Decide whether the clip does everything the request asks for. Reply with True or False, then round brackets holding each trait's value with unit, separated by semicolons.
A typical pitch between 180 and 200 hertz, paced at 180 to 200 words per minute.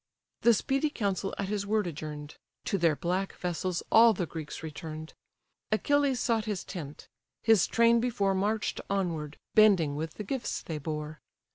False (190 Hz; 155 wpm)